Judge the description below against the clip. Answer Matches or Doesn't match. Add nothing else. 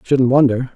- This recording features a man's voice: Matches